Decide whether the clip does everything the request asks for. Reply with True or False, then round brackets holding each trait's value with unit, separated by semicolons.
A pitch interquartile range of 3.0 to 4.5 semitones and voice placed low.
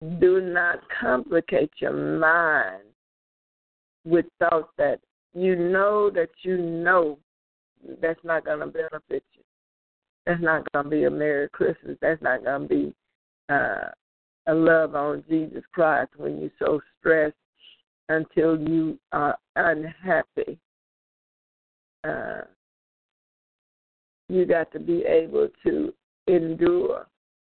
False (3.7 semitones; 165 Hz)